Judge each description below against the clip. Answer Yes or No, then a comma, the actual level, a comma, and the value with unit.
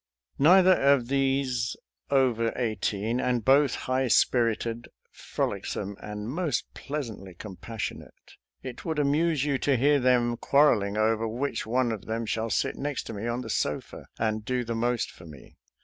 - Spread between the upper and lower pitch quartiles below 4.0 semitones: Yes, average, 3.6 semitones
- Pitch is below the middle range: Yes, low, 120 Hz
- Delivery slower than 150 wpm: No, average, 155 wpm